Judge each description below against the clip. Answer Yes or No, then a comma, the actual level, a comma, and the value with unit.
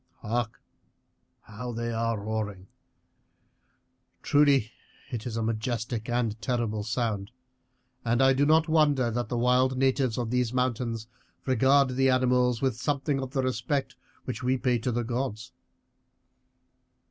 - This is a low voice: Yes, low, 125 Hz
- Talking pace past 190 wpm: No, slow, 135 wpm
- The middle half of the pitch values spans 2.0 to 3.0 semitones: Yes, narrow, 2.4 semitones